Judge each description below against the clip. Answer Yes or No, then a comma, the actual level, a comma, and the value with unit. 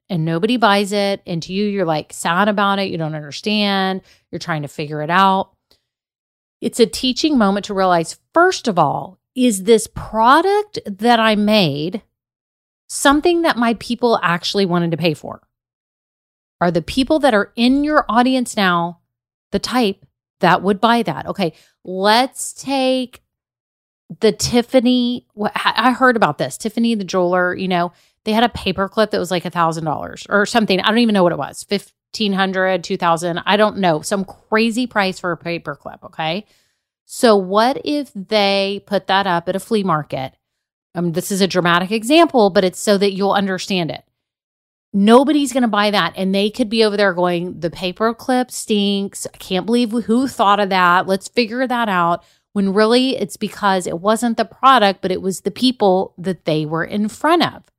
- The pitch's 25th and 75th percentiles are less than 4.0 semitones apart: No, average, 4.5 semitones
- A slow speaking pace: No, average, 180 wpm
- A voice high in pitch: Yes, high, 200 Hz